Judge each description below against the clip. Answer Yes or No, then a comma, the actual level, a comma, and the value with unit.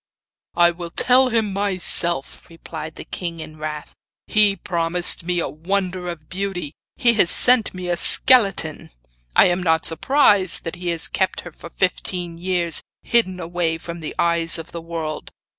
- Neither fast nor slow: Yes, average, 165 wpm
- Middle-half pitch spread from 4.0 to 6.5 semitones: No, narrow, 2.4 semitones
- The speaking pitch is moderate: Yes, medium, 175 Hz